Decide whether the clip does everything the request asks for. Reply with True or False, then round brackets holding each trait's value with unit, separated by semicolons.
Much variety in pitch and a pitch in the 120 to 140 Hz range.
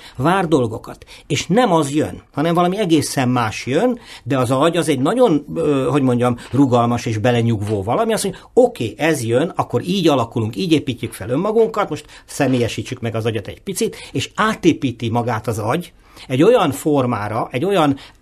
True (5.7 semitones; 135 Hz)